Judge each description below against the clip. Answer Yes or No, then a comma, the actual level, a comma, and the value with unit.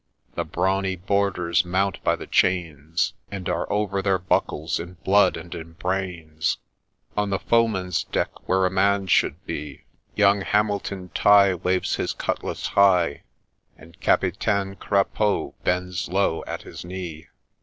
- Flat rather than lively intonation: Yes, narrow, 2.3 semitones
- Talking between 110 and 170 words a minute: Yes, average, 145 wpm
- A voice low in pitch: Yes, very low, 95 Hz